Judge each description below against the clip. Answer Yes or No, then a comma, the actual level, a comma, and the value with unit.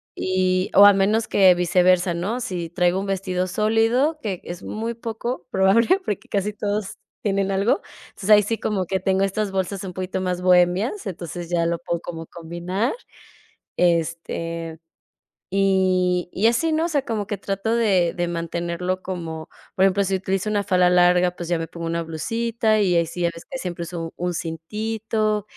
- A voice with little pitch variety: No, average, 3.1 semitones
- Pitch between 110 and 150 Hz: No, medium, 185 Hz